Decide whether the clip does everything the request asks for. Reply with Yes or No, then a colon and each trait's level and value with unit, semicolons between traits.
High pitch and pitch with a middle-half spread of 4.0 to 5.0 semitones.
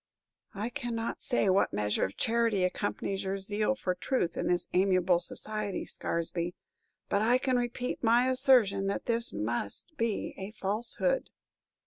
Yes: high, 205 Hz; average, 4.5 semitones